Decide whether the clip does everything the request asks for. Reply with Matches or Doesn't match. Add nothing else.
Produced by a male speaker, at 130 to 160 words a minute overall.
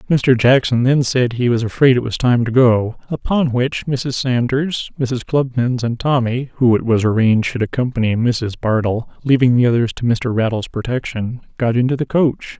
Doesn't match